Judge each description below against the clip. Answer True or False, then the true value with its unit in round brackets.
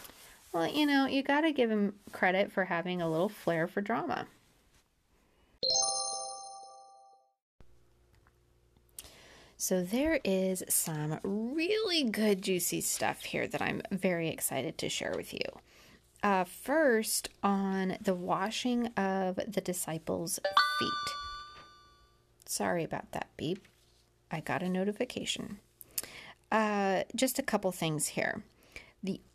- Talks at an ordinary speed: False (115 wpm)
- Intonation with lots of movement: True (7.0 semitones)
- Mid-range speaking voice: False (195 Hz)